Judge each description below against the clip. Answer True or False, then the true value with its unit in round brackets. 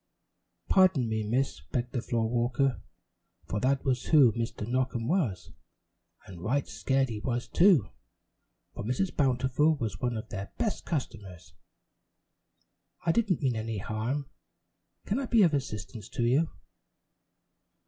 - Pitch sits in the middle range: False (125 Hz)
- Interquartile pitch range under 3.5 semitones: False (4.2 semitones)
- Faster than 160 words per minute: False (140 wpm)